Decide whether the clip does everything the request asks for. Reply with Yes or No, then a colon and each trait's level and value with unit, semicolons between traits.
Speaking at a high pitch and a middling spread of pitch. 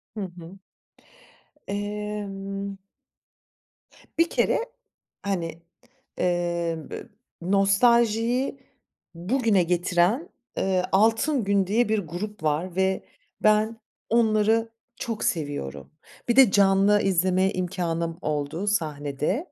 Yes: high, 195 Hz; average, 3.8 semitones